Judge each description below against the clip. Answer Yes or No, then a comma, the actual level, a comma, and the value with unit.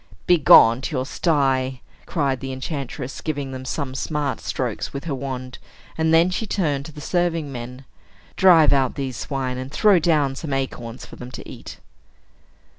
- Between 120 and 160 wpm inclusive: No, average, 170 wpm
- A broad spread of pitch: No, average, 3.4 semitones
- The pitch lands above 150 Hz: No, medium, 140 Hz